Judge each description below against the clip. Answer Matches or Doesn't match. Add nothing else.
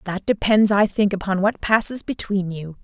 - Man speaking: Doesn't match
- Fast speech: Doesn't match